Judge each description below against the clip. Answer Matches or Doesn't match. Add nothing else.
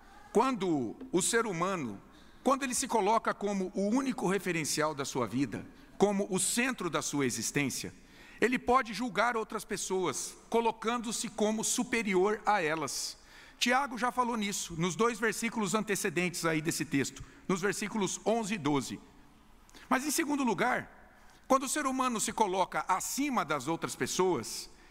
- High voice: Matches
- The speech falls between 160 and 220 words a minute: Doesn't match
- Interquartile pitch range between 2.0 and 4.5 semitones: Doesn't match